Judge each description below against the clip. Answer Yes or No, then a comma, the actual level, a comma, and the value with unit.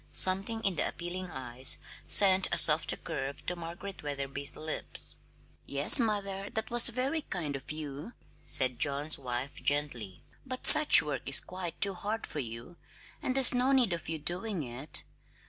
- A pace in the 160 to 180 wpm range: Yes, average, 165 wpm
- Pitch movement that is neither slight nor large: No, wide, 6.3 semitones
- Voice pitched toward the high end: No, medium, 170 Hz